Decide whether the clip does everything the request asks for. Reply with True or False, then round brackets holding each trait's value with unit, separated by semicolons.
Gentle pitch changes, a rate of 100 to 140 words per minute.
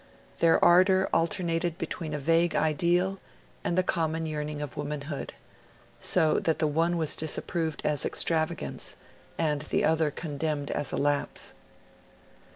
True (2.1 semitones; 135 wpm)